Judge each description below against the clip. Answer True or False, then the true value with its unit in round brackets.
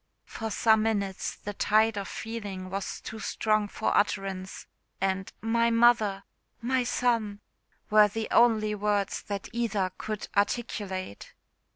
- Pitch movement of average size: False (2.3 semitones)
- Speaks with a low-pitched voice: False (210 Hz)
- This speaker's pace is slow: True (130 wpm)